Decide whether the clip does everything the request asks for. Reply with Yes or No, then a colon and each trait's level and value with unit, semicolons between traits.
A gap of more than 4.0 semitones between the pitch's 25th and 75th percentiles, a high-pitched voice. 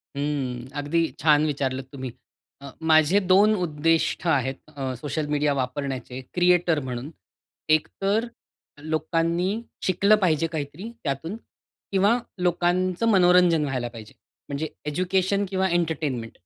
No: average, 4.4 semitones; medium, 155 Hz